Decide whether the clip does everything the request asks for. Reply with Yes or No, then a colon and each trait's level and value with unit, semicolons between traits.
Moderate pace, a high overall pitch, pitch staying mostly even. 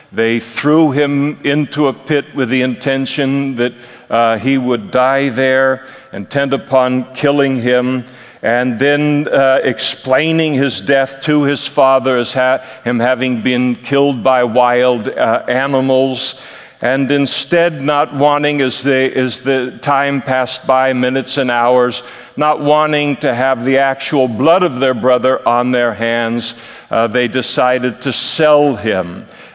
No: average, 145 wpm; low, 130 Hz; narrow, 2.0 semitones